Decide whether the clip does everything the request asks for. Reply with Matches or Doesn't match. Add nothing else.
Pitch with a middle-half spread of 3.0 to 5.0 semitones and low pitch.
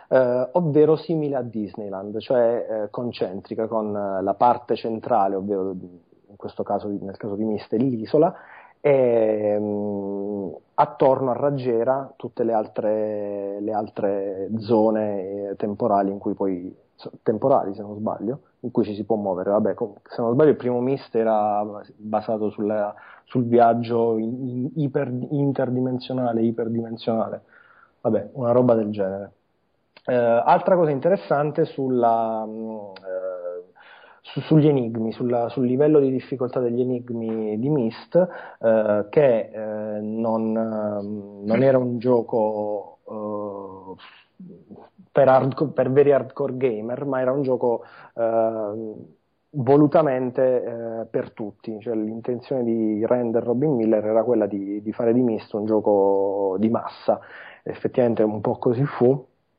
Matches